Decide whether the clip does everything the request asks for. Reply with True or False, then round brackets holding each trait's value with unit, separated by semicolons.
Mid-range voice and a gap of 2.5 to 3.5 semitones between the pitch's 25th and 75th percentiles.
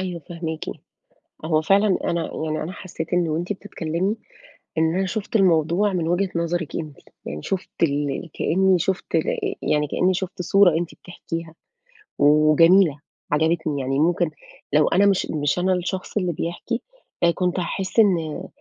True (175 Hz; 3.0 semitones)